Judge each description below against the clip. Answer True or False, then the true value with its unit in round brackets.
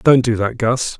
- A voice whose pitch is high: False (120 Hz)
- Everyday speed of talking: False (240 wpm)